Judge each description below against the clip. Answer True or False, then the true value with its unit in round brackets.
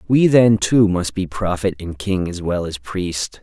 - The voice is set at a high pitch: False (95 Hz)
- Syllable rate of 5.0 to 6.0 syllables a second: False (4.0 syllables/s)